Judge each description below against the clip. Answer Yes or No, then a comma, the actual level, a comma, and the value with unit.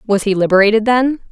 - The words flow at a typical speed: Yes, average, 185 wpm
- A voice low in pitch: No, high, 215 Hz